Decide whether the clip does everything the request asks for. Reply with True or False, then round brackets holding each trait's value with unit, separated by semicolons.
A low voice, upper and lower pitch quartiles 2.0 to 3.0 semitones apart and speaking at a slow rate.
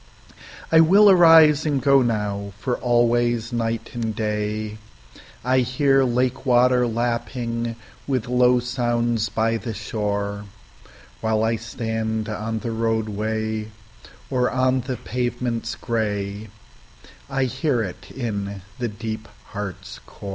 True (115 Hz; 2.5 semitones; 110 wpm)